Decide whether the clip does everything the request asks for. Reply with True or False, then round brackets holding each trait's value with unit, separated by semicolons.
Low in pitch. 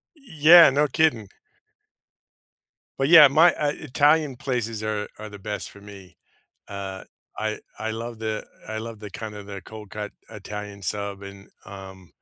True (110 Hz)